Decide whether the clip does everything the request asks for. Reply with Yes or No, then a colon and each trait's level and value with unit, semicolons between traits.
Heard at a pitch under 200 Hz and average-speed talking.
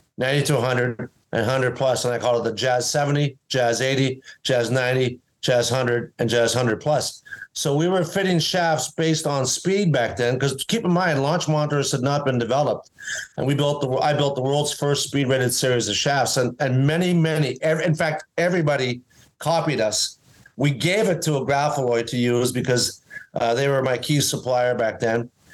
Yes: low, 135 Hz; average, 195 wpm